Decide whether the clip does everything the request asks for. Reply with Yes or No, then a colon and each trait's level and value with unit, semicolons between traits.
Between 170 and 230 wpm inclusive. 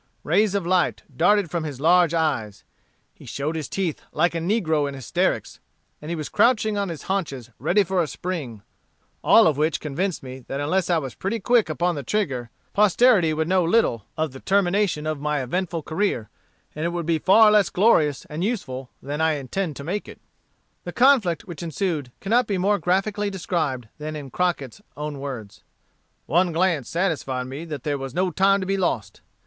Yes: average, 190 wpm